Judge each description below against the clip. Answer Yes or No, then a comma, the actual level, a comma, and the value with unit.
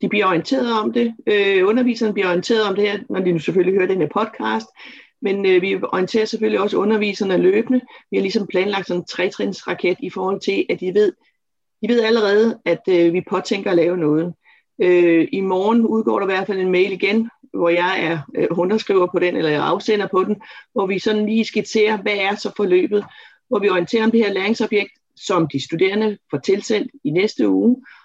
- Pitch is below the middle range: No, high, 200 Hz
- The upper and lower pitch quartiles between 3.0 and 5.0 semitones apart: Yes, average, 3.4 semitones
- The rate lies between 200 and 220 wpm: Yes, average, 205 wpm